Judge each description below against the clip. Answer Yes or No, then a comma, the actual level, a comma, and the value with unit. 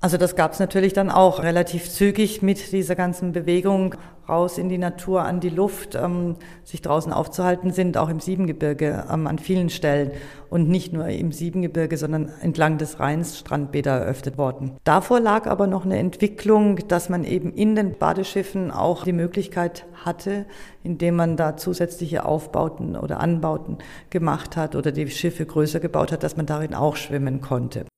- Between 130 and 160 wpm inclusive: No, average, 175 wpm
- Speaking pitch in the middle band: Yes, medium, 175 Hz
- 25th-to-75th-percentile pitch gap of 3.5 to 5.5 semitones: No, average, 2.9 semitones